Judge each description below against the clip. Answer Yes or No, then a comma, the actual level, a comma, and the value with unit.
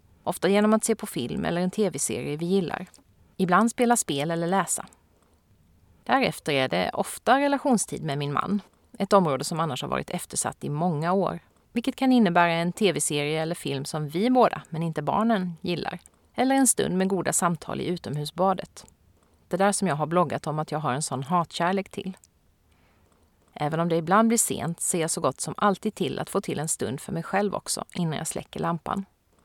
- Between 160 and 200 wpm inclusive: Yes, fast, 195 wpm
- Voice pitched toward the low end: No, medium, 175 Hz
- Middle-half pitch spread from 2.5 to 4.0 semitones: No, average, 5.3 semitones